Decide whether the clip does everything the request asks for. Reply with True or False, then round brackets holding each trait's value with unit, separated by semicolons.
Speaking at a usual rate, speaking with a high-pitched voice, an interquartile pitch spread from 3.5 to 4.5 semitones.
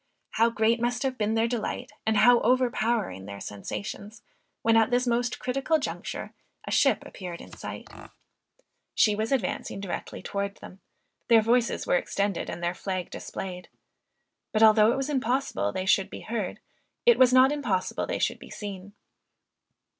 True (160 wpm; 225 Hz; 3.9 semitones)